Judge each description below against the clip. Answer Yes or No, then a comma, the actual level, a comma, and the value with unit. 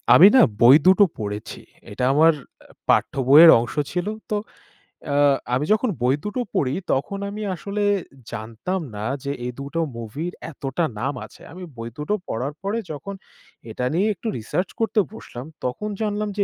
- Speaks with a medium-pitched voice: Yes, medium, 155 Hz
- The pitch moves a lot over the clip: Yes, wide, 8.1 semitones